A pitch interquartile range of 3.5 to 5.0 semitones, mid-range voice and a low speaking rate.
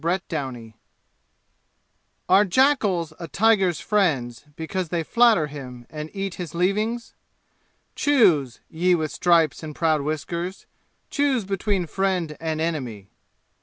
Yes: average, 4.2 semitones; medium, 170 Hz; slow, 120 wpm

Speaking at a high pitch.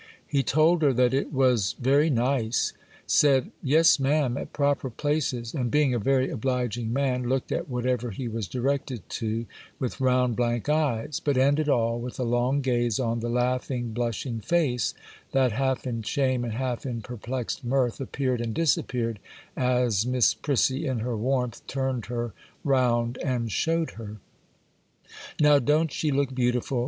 No: low, 125 Hz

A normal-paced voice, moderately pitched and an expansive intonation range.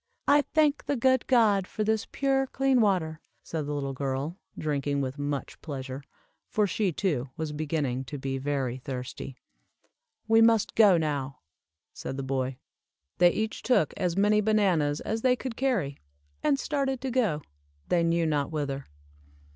Yes: average, 160 wpm; medium, 165 Hz; wide, 8.1 semitones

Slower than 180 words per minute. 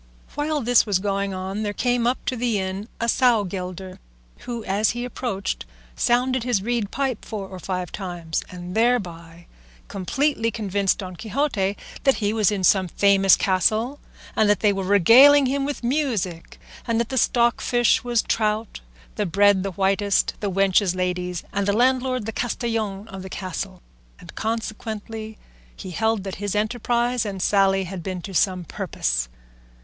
Yes: average, 165 wpm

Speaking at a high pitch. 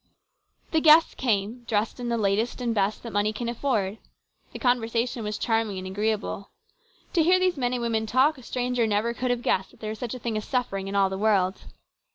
Yes: high, 225 Hz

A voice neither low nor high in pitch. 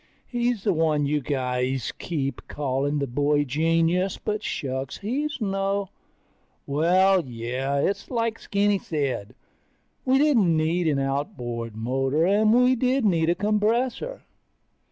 Yes: medium, 165 Hz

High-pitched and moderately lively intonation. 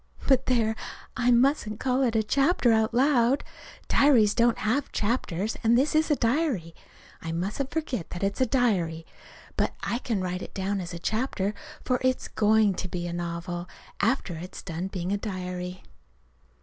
No: high, 220 Hz; wide, 5.7 semitones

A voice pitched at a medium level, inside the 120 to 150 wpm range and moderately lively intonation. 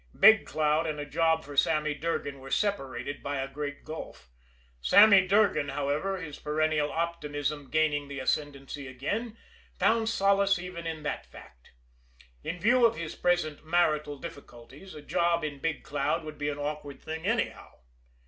No: medium, 155 Hz; average, 160 wpm; average, 3.3 semitones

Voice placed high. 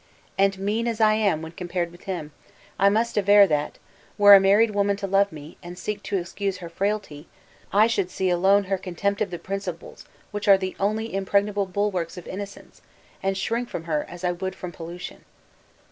Yes: high, 195 Hz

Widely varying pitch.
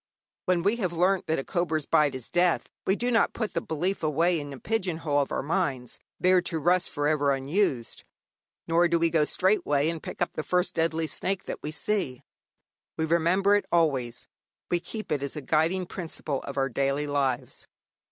No: average, 4.0 semitones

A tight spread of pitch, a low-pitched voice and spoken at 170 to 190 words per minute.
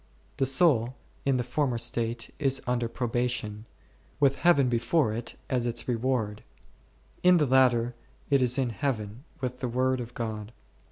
No: narrow, 2.3 semitones; low, 125 Hz; average, 160 wpm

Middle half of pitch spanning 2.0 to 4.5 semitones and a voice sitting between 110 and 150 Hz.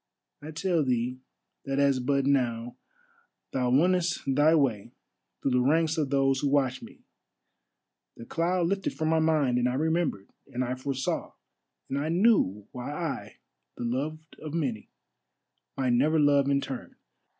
Yes: average, 3.9 semitones; medium, 140 Hz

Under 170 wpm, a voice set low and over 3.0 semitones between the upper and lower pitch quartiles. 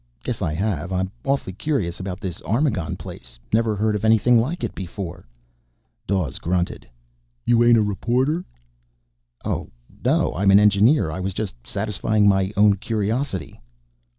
Yes: average, 150 wpm; low, 100 Hz; average, 3.5 semitones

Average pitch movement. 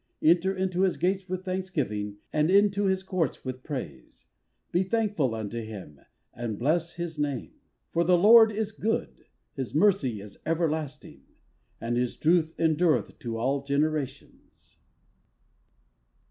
No: wide, 6.5 semitones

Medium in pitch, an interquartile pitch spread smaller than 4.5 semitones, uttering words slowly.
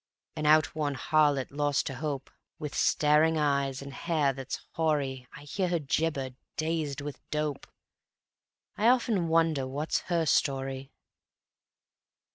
Yes: medium, 150 Hz; average, 2.7 semitones; slow, 125 wpm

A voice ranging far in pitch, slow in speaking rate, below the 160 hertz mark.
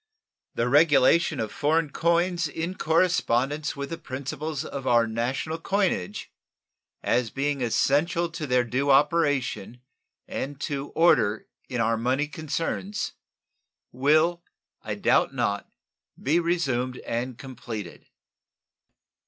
No: average, 4.7 semitones; slow, 110 wpm; medium, 140 Hz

